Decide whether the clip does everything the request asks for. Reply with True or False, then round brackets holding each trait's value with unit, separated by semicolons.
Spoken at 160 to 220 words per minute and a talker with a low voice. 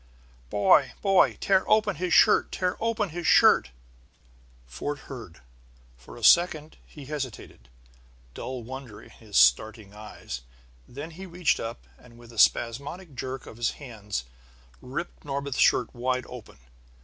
False (140 wpm; 130 Hz)